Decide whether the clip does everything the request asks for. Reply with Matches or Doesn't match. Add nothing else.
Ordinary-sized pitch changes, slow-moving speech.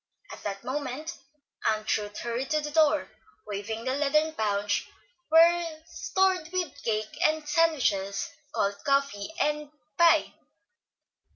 Doesn't match